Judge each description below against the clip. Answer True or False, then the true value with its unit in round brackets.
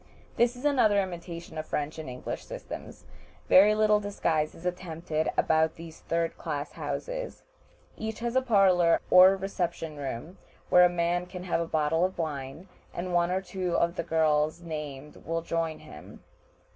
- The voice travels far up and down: False (3.0 semitones)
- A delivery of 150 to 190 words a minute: True (170 wpm)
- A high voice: False (170 Hz)